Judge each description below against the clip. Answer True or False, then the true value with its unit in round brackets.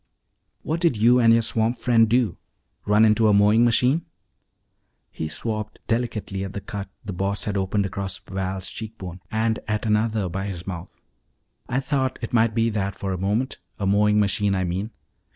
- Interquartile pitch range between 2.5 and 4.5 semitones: True (2.8 semitones)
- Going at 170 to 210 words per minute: True (185 wpm)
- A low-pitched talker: True (105 Hz)